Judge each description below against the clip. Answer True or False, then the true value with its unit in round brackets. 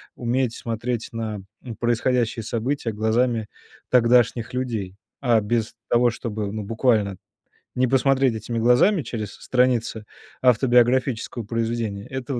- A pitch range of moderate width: False (2.2 semitones)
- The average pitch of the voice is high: False (120 Hz)